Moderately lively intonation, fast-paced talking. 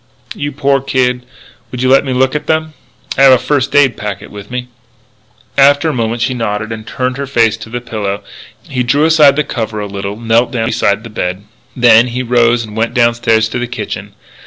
Yes: average, 3.1 semitones; fast, 210 wpm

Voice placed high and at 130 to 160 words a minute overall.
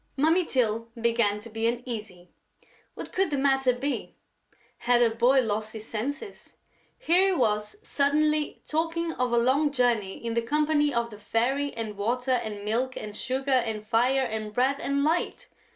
No: high, 245 Hz; average, 170 wpm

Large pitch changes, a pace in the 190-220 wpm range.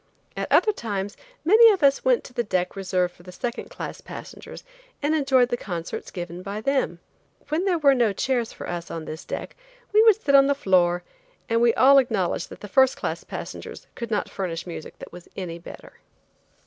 Yes: wide, 7.4 semitones; average, 200 wpm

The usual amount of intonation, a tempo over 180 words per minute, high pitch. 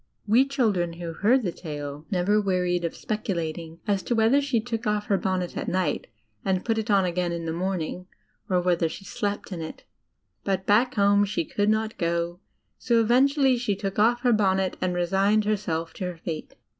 Yes: average, 3.8 semitones; average, 195 wpm; high, 195 Hz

